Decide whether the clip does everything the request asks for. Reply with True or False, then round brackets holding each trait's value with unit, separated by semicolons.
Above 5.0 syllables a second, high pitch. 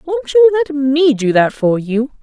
False (3.9 syllables/s; 270 Hz)